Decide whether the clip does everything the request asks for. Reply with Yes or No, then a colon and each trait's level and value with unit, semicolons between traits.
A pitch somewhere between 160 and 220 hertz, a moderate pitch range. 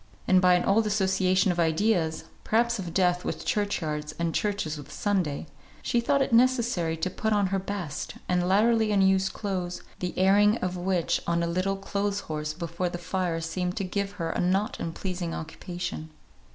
Yes: medium, 185 Hz; average, 3.0 semitones